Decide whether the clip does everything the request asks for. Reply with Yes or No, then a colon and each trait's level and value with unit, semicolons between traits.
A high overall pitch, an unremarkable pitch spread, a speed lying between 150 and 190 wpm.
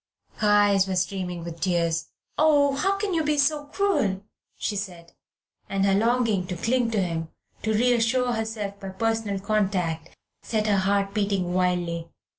Yes: high, 200 Hz; average, 4.1 semitones; average, 160 wpm